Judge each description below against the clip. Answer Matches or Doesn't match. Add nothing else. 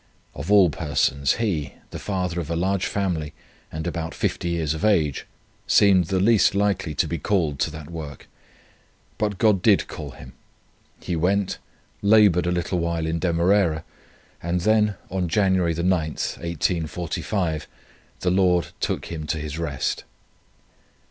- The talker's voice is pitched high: Doesn't match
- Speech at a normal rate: Matches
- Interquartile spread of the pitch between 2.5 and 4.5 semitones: Matches